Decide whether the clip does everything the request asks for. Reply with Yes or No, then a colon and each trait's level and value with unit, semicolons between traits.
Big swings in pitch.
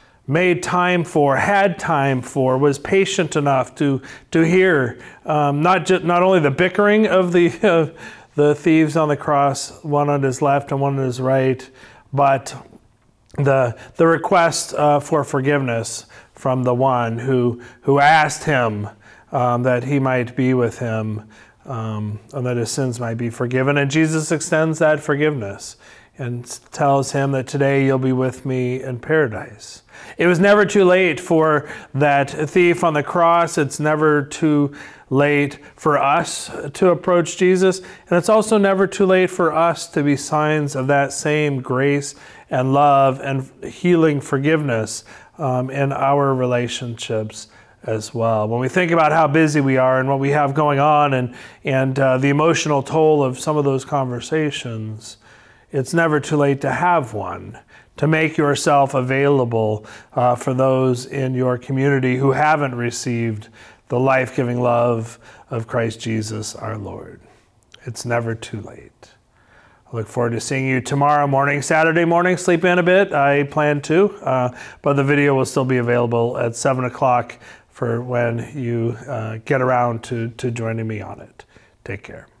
No: average, 3.9 semitones